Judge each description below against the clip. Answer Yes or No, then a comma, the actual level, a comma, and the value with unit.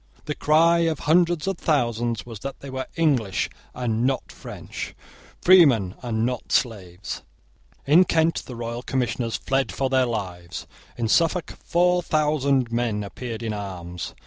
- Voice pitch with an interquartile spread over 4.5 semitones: Yes, wide, 5.4 semitones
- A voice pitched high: No, low, 125 Hz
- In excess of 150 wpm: No, average, 145 wpm